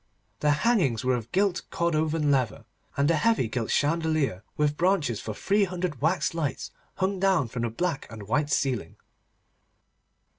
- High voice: No, medium, 150 Hz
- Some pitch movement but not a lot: No, wide, 6.1 semitones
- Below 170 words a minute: Yes, average, 155 wpm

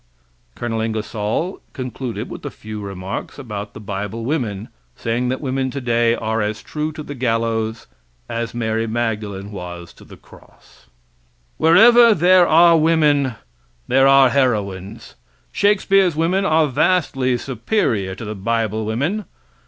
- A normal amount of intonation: No, wide, 5.7 semitones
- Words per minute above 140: No, slow, 135 wpm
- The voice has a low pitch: Yes, low, 120 Hz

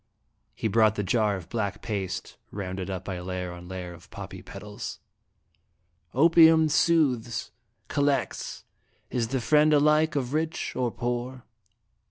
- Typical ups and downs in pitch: No, wide, 7.5 semitones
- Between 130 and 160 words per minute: Yes, average, 140 wpm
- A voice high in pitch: No, low, 115 Hz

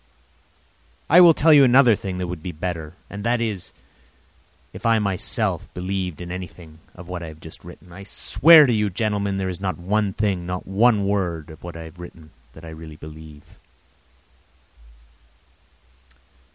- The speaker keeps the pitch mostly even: No, average, 3.8 semitones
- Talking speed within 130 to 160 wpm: No, average, 170 wpm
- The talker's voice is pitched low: Yes, very low, 90 Hz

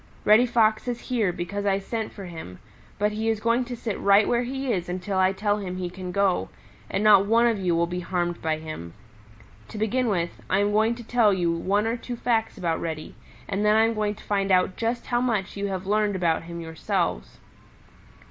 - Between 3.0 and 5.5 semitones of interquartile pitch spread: Yes, average, 3.8 semitones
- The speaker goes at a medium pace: No, fast, 225 wpm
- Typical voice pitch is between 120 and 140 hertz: No, high, 200 Hz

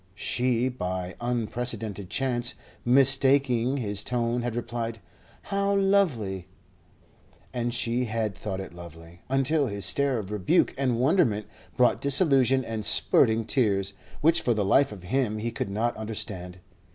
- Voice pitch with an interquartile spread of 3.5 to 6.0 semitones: Yes, average, 4.2 semitones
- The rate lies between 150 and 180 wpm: No, average, 140 wpm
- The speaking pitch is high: No, low, 120 Hz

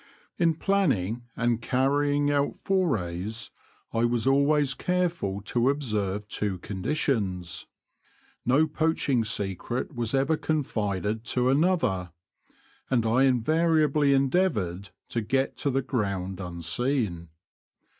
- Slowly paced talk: Yes, slow, 105 wpm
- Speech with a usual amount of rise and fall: No, wide, 6.1 semitones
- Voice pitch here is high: No, low, 125 Hz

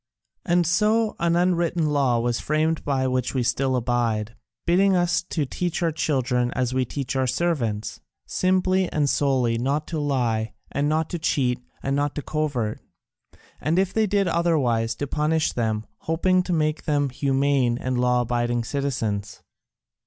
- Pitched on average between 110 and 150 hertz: Yes, medium, 140 Hz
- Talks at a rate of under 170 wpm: Yes, average, 160 wpm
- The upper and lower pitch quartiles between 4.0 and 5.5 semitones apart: Yes, average, 5.2 semitones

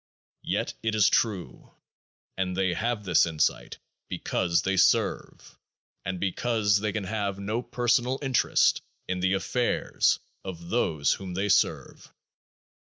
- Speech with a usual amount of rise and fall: Yes, average, 3.4 semitones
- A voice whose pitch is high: No, low, 100 Hz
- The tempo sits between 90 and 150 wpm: Yes, slow, 135 wpm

